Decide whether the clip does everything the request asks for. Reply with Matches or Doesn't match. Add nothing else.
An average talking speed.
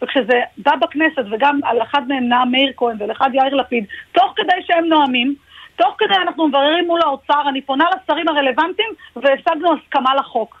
Doesn't match